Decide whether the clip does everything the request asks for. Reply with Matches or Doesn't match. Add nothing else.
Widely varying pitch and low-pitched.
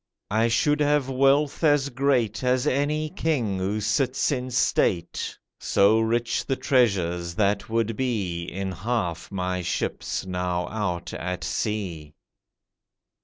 Matches